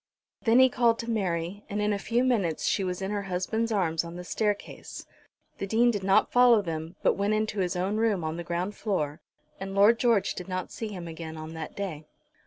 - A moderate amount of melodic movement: Yes, average, 4.0 semitones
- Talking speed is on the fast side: Yes, fast, 220 wpm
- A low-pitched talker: No, high, 195 Hz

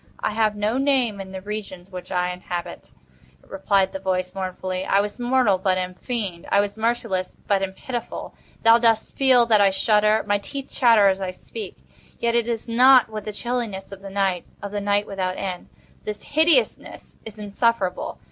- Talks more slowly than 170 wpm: No, average, 185 wpm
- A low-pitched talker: No, high, 205 Hz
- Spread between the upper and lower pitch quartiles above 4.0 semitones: No, average, 3.5 semitones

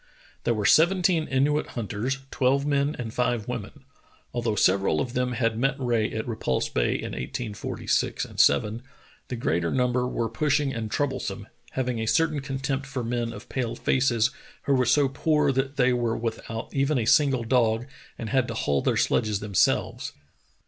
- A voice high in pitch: No, low, 125 Hz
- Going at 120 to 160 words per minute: No, average, 175 wpm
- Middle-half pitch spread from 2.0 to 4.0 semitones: Yes, average, 3.3 semitones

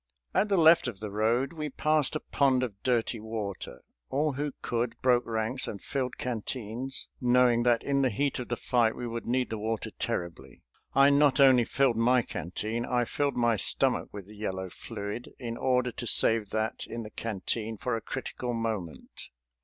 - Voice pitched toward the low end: Yes, low, 120 Hz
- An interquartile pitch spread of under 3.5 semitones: Yes, average, 2.9 semitones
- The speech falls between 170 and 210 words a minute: Yes, average, 185 wpm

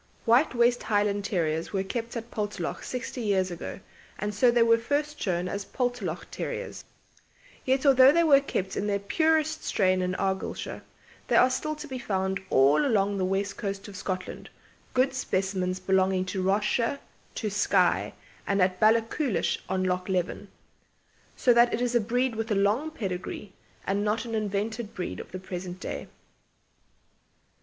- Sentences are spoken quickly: No, average, 165 wpm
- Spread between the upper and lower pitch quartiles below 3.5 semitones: No, average, 4.3 semitones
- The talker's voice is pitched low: No, high, 205 Hz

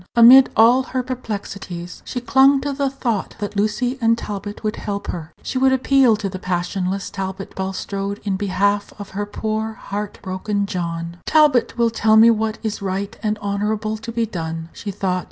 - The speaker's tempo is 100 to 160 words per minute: No, average, 175 wpm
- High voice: Yes, high, 210 Hz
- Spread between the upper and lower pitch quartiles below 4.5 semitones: Yes, average, 3.0 semitones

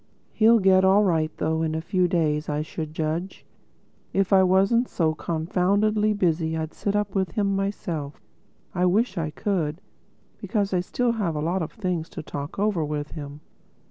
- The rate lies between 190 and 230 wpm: No, average, 175 wpm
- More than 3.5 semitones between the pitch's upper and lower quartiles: Yes, average, 4.0 semitones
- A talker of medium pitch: Yes, medium, 180 Hz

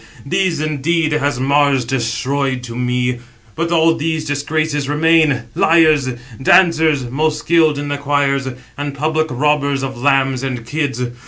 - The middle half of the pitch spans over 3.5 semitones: No, average, 2.8 semitones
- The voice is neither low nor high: Yes, medium, 145 Hz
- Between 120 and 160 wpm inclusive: Yes, average, 145 wpm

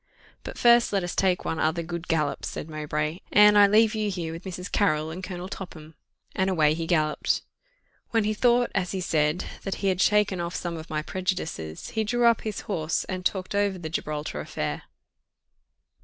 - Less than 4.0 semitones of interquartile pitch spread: No, average, 4.3 semitones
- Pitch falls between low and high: Yes, medium, 180 Hz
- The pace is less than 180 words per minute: No, average, 195 wpm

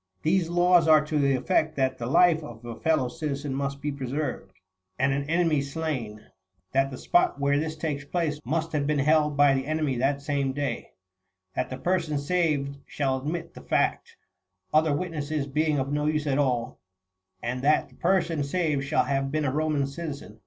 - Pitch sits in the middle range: Yes, medium, 145 Hz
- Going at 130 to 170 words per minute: No, average, 190 wpm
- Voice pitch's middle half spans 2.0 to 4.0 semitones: Yes, narrow, 2.4 semitones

